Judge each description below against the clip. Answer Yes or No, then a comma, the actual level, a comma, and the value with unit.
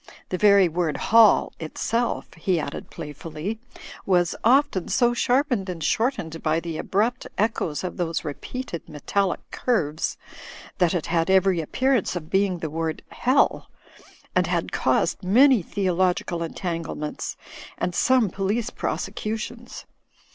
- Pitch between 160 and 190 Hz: Yes, medium, 185 Hz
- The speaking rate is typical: No, slow, 130 wpm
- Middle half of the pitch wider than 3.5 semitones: Yes, wide, 5.6 semitones